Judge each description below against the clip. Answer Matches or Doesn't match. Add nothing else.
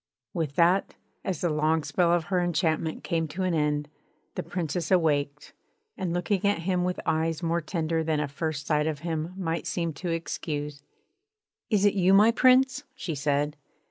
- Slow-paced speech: Doesn't match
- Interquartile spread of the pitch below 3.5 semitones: Matches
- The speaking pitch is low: Doesn't match